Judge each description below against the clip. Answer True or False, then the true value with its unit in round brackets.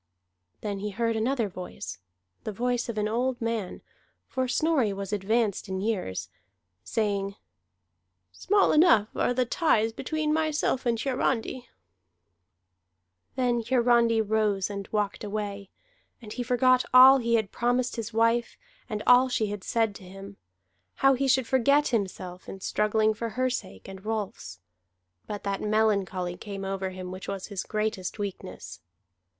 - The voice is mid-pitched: False (220 Hz)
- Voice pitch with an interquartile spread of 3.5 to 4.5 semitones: True (3.8 semitones)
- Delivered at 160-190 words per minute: False (145 wpm)